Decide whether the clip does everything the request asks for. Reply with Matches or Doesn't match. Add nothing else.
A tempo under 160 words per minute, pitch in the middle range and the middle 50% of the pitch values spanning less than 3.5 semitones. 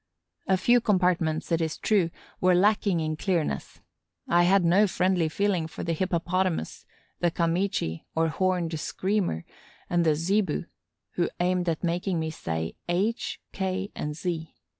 Matches